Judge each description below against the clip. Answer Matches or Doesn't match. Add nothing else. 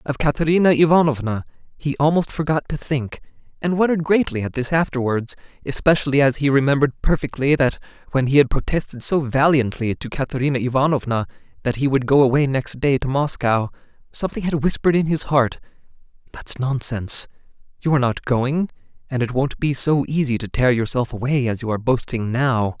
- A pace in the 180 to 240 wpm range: Doesn't match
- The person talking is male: Matches